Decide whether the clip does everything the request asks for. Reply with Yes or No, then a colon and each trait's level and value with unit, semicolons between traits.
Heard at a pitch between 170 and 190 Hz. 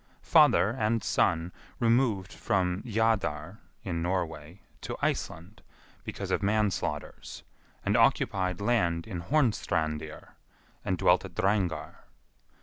No: very low, 95 Hz